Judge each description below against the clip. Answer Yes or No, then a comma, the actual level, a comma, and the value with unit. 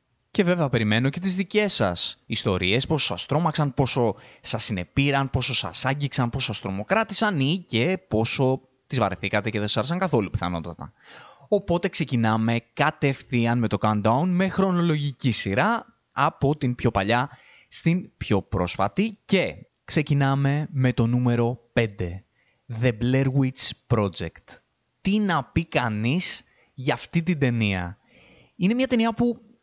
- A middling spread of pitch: No, wide, 6.1 semitones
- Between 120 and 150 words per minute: Yes, average, 140 wpm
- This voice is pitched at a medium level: No, low, 130 Hz